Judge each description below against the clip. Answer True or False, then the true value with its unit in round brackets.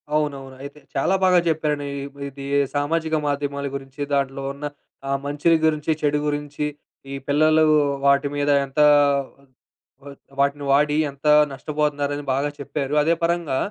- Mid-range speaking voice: True (145 Hz)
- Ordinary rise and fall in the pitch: False (1.3 semitones)